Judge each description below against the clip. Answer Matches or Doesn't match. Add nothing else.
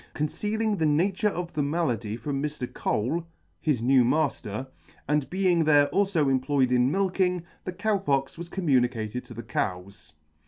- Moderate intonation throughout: Doesn't match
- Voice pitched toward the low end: Doesn't match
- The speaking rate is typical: Matches